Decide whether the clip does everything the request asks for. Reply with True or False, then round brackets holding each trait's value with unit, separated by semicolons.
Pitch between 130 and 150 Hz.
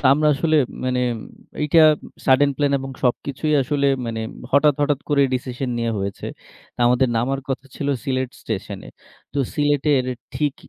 True (135 Hz)